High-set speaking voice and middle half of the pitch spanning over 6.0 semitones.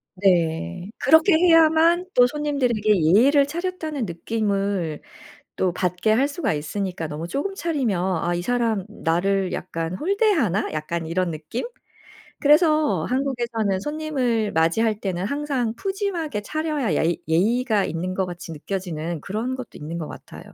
Yes: high, 215 Hz; wide, 8.8 semitones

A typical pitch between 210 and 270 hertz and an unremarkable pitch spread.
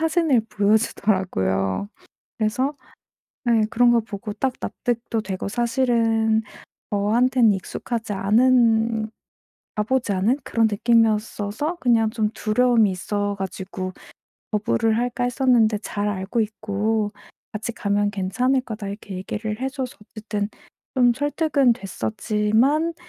Yes: high, 220 Hz; average, 3.0 semitones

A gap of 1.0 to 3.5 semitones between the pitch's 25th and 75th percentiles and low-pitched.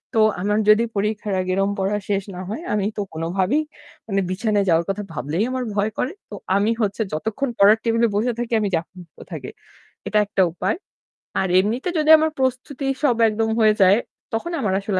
No: average, 3.0 semitones; high, 210 Hz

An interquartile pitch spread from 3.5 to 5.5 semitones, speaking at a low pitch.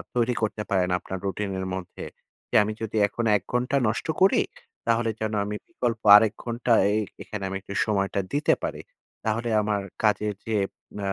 No: average, 2.7 semitones; low, 110 Hz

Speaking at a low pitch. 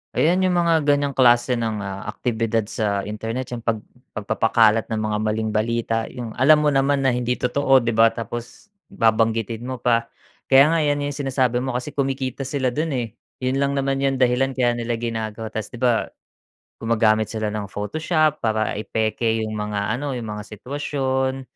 Yes: low, 120 Hz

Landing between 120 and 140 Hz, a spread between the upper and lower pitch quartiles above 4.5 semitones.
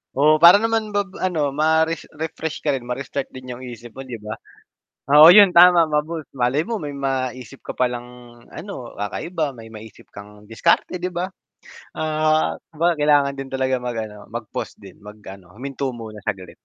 Yes: low, 135 Hz; average, 4.9 semitones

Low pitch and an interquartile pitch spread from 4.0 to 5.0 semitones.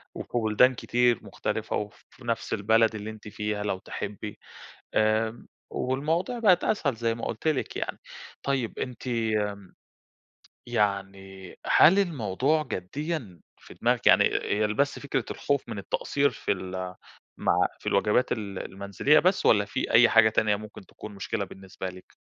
Yes: low, 110 Hz; average, 4.4 semitones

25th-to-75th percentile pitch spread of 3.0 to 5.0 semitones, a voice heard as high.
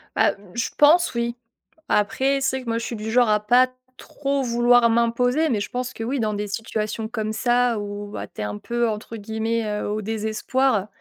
No: narrow, 2.5 semitones; high, 230 Hz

